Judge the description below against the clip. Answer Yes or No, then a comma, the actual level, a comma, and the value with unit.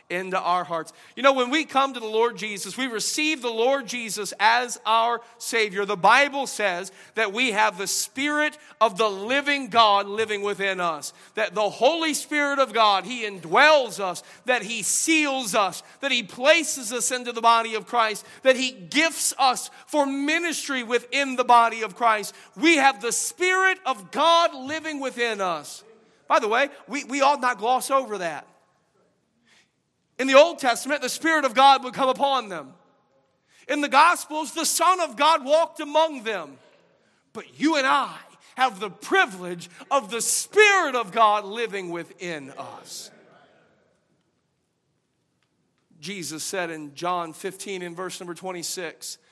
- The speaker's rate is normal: Yes, average, 160 wpm